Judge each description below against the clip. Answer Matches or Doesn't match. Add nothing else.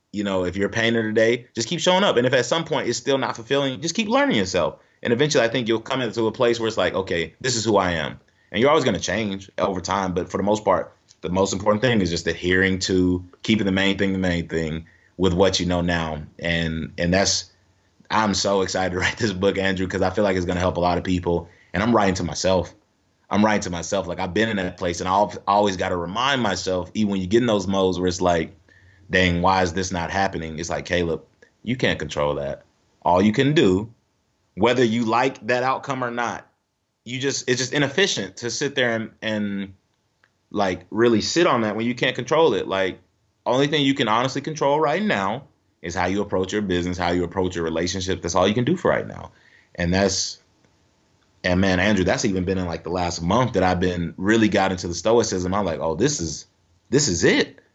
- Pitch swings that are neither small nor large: Matches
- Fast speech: Matches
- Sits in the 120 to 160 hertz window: Doesn't match